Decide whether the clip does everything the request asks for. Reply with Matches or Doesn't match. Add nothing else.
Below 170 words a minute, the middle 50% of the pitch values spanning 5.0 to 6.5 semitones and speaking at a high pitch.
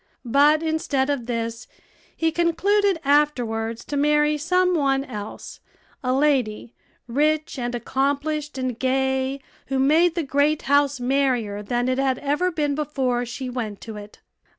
Doesn't match